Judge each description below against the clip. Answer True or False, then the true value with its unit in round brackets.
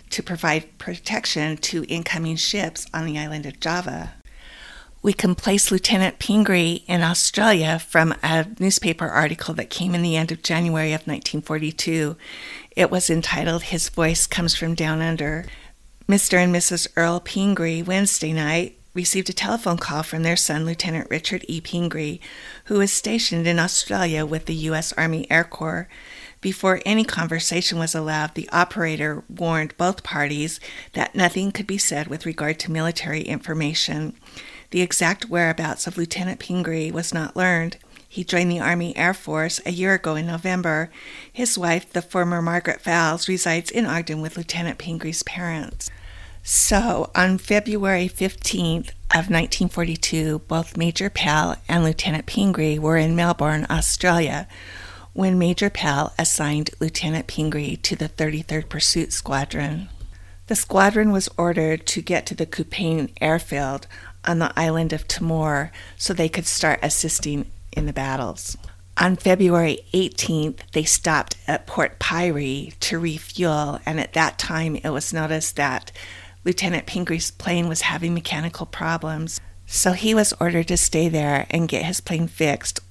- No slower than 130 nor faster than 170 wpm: True (150 wpm)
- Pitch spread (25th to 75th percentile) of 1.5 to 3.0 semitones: True (2.5 semitones)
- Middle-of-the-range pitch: True (165 Hz)